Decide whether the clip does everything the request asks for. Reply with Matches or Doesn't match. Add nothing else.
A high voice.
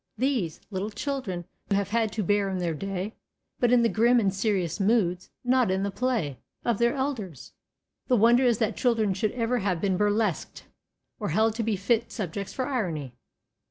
Matches